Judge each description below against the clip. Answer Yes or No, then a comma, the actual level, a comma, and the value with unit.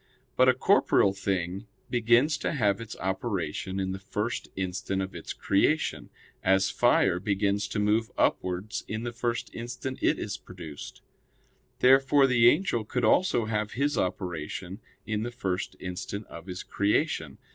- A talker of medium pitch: No, low, 105 Hz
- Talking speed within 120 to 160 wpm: Yes, average, 150 wpm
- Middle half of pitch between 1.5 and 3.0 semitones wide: No, average, 4.0 semitones